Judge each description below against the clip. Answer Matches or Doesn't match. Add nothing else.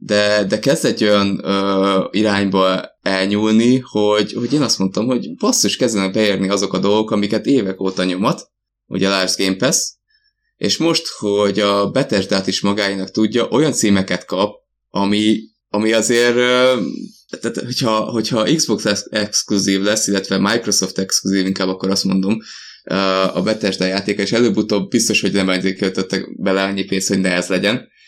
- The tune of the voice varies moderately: Doesn't match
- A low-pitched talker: Matches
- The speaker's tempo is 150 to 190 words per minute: Matches